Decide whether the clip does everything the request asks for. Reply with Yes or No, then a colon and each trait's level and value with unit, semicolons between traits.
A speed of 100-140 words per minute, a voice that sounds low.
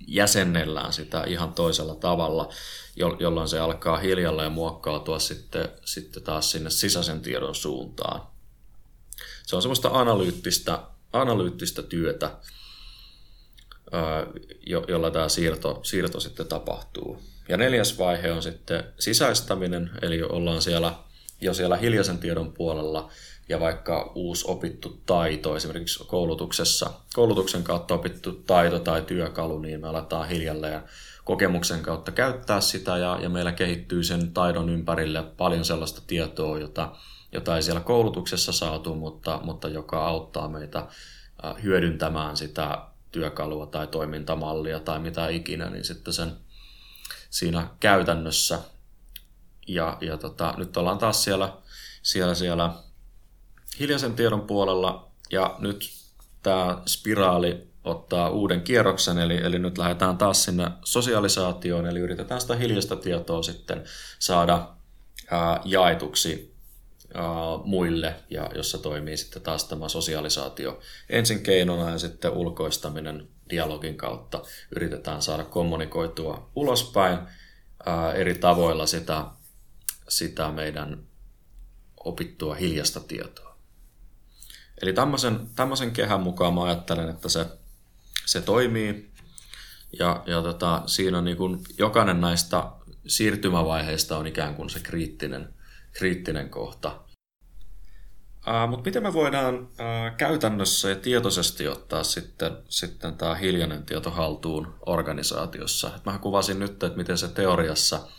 Yes: average, 115 wpm; very low, 85 Hz